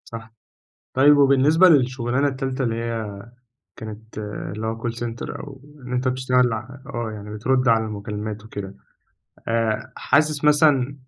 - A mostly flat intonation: No, average, 3.4 semitones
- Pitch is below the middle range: Yes, low, 120 Hz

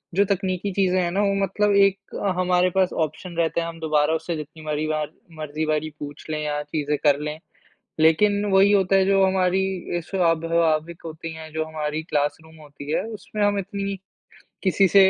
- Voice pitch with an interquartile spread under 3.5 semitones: No, average, 3.8 semitones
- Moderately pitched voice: Yes, medium, 165 Hz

